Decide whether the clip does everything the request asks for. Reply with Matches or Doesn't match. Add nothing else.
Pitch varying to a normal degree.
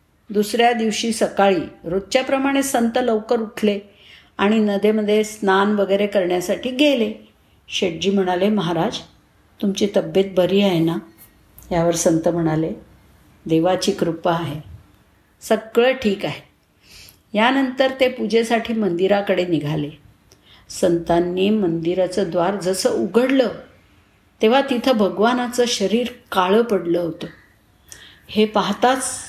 Matches